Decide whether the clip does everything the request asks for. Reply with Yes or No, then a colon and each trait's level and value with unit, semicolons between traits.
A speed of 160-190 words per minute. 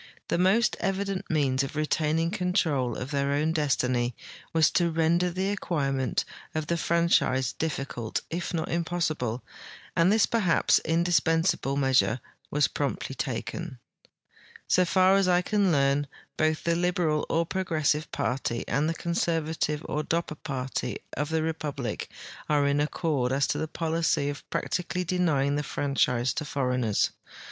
No: average, 145 wpm